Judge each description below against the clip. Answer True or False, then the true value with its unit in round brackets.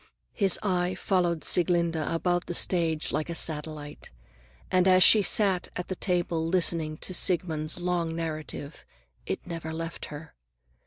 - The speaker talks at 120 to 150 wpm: True (145 wpm)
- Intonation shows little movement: True (2.2 semitones)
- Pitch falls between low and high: True (170 Hz)